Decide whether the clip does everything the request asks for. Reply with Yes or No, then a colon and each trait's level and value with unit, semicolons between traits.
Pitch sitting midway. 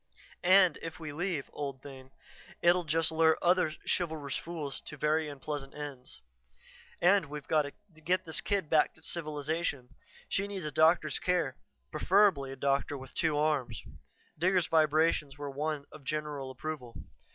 Yes: medium, 155 Hz